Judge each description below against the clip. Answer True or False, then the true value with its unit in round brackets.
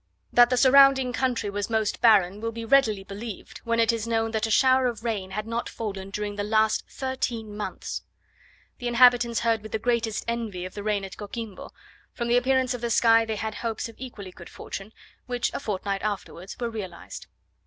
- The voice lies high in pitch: True (225 Hz)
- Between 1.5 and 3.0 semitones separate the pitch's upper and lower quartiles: True (2.6 semitones)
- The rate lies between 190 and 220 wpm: True (200 wpm)